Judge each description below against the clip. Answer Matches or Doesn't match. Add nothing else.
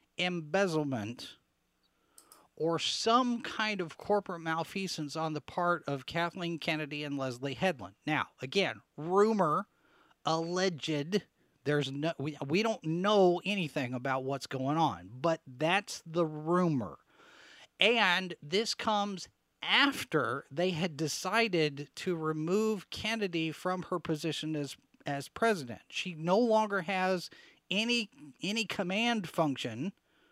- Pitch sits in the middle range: Matches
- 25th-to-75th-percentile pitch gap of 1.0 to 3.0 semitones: Doesn't match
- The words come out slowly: Matches